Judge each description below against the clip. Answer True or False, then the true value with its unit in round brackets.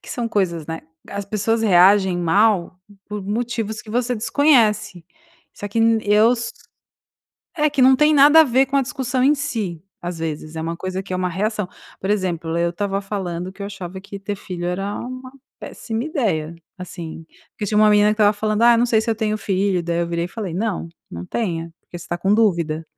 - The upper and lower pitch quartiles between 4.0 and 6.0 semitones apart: True (4.4 semitones)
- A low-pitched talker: False (205 Hz)